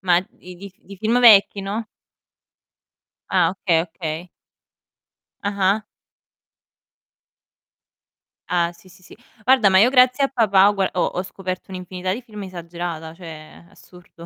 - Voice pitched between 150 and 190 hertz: Yes, medium, 185 Hz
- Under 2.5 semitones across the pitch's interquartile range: No, average, 2.8 semitones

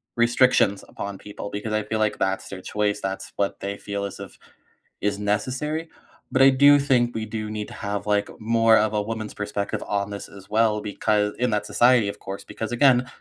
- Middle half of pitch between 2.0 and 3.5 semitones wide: Yes, average, 2.7 semitones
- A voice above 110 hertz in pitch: No, low, 105 Hz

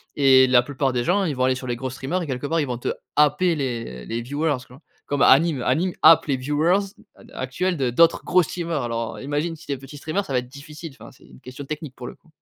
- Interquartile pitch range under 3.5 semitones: No, average, 3.9 semitones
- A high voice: No, medium, 140 Hz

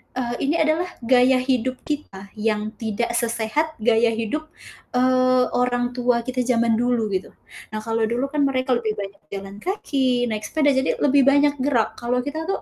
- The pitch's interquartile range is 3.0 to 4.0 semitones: Yes, average, 3.3 semitones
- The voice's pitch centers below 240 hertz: No, very high, 250 Hz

